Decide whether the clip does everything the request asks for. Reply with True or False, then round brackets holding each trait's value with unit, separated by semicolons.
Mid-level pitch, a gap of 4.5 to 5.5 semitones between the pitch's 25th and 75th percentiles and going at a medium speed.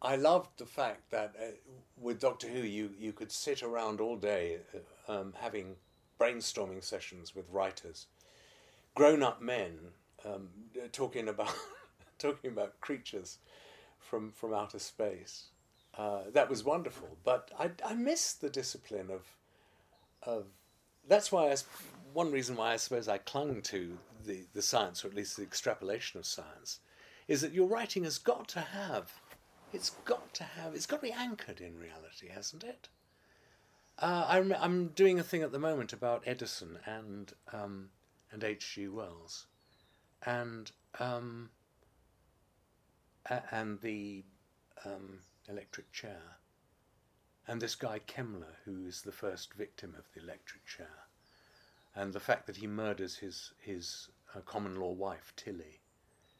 False (110 Hz; 5.2 semitones; 150 wpm)